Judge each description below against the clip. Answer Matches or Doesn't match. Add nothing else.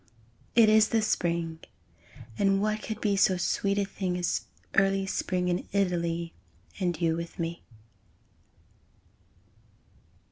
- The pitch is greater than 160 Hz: Matches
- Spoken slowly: Matches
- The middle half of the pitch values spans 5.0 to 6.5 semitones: Doesn't match